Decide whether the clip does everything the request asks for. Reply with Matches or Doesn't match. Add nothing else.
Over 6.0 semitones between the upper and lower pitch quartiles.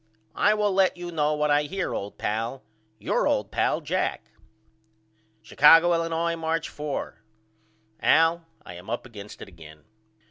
Matches